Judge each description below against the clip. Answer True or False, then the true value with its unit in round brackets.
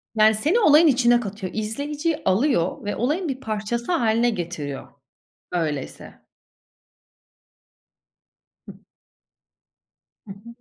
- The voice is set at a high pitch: True (225 Hz)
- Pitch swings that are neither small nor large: False (6.3 semitones)